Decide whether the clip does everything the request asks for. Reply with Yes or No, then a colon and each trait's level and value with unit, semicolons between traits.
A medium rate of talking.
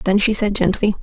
No: fast, 235 wpm